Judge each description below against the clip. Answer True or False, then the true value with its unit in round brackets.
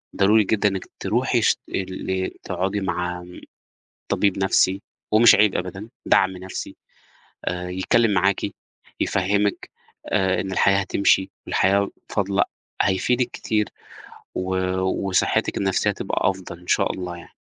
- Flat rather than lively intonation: True (1.4 semitones)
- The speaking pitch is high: False (95 Hz)